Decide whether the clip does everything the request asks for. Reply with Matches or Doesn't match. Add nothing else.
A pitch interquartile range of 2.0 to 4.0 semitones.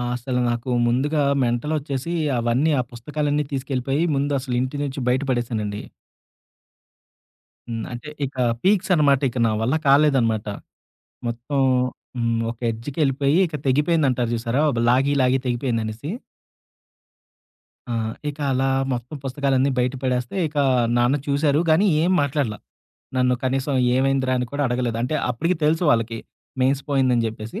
Matches